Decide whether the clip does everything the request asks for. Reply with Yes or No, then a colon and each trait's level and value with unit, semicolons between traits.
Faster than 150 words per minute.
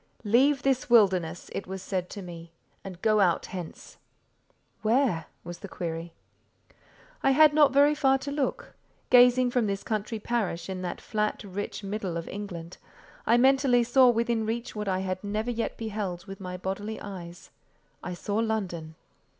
Yes: average, 160 wpm